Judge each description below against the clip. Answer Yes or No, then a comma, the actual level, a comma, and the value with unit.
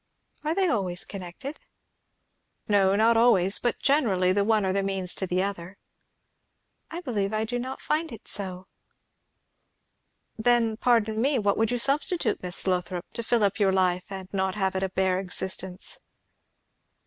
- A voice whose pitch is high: Yes, high, 200 Hz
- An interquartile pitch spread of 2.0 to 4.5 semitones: Yes, average, 3.9 semitones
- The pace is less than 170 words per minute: Yes, average, 160 wpm